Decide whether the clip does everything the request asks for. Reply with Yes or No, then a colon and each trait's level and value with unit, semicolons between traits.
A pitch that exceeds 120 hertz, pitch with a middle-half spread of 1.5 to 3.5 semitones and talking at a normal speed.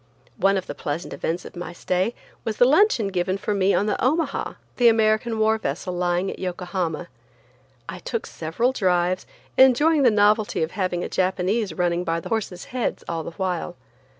No: high, 190 Hz; average, 4.0 semitones; average, 180 wpm